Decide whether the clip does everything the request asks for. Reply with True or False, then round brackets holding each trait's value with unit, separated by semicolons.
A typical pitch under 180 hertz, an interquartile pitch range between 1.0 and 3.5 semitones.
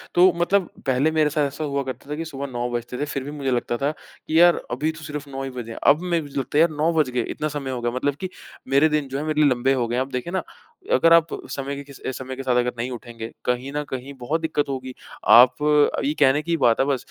True (140 Hz; 3.2 semitones)